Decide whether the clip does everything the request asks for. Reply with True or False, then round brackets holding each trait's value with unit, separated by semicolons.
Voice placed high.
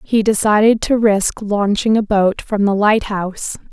True (210 Hz)